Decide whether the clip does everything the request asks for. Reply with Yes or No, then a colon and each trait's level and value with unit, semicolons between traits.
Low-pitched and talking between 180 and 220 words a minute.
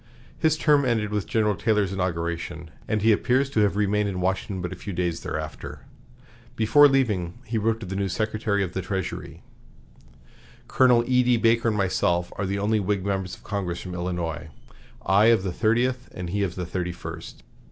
Yes: low, 100 Hz; average, 185 wpm